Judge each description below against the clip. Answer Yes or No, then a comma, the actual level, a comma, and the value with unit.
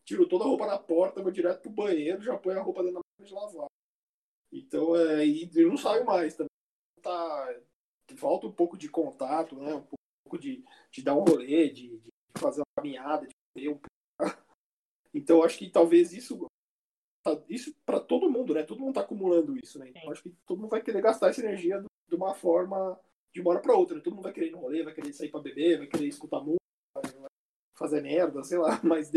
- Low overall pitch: No, medium, 185 Hz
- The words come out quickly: Yes, fast, 210 wpm